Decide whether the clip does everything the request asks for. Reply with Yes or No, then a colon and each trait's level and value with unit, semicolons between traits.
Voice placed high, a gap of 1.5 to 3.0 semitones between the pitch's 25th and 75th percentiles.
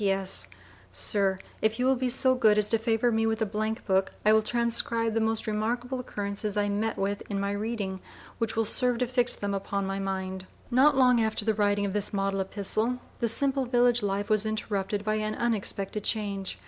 Yes: high, 215 Hz; average, 2.7 semitones